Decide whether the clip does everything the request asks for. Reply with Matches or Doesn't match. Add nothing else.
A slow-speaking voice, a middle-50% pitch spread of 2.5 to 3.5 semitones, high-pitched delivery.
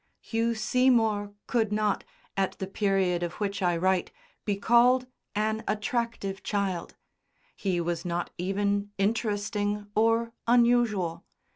Matches